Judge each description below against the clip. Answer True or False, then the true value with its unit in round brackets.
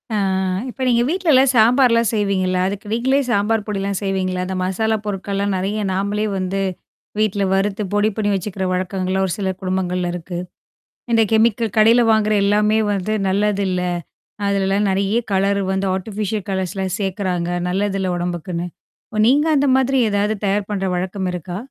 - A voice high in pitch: True (200 Hz)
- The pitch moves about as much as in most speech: False (2.3 semitones)